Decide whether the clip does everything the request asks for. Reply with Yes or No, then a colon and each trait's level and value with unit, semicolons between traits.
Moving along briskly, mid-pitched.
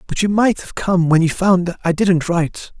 Yes: fast, 235 wpm; medium, 180 Hz